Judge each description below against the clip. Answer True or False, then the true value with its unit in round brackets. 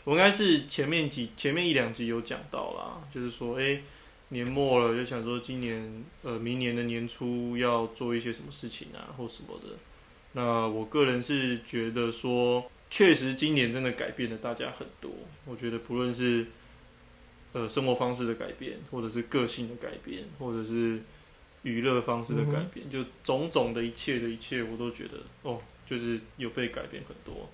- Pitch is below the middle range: True (120 Hz)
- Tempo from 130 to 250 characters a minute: False (270 characters per minute)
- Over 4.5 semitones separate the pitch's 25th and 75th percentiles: False (1.6 semitones)